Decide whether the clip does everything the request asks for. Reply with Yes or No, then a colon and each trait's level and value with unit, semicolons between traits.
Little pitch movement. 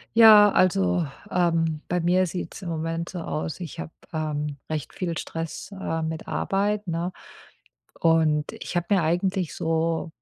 Yes: narrow, 2.3 semitones